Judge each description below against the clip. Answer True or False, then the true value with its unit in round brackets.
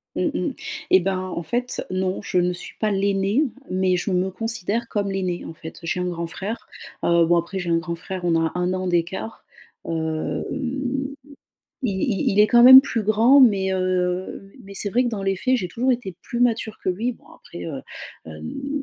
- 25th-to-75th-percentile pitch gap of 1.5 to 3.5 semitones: False (4.0 semitones)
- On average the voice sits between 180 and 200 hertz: True (190 Hz)